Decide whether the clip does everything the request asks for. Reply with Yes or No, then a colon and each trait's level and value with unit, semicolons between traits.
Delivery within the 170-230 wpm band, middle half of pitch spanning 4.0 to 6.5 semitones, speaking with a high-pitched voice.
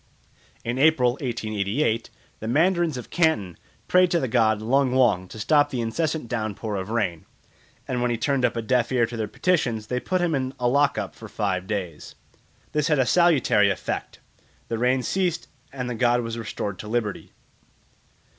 No: average, 180 wpm; average, 4.4 semitones; low, 120 Hz